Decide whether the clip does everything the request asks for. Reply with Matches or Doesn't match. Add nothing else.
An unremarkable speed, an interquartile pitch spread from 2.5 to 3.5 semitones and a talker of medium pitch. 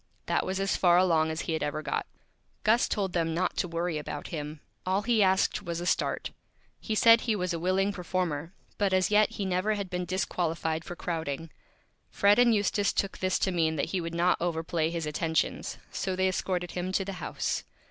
Doesn't match